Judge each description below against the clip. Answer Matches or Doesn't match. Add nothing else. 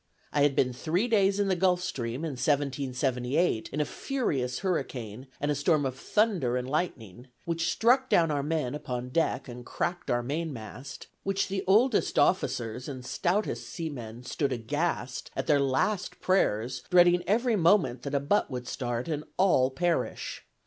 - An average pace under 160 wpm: Doesn't match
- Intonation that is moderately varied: Doesn't match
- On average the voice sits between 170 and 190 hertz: Doesn't match